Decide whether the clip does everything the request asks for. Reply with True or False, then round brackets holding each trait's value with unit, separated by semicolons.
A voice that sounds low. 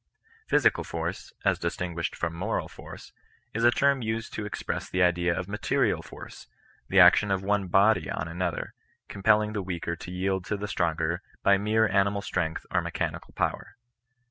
True (95 Hz)